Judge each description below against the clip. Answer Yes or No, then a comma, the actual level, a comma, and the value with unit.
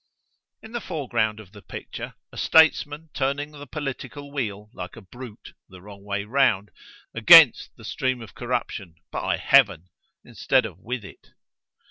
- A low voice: Yes, low, 120 Hz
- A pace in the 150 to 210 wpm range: No, average, 140 wpm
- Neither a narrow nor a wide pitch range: No, wide, 5.8 semitones